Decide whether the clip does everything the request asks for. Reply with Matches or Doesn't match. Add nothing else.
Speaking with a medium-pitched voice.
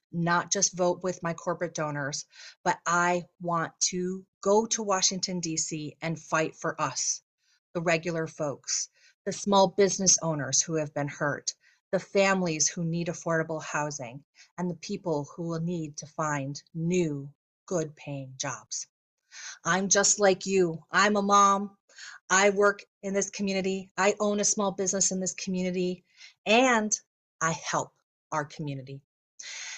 Matches